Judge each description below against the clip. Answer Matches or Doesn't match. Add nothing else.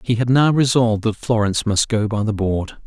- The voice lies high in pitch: Doesn't match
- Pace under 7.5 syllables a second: Matches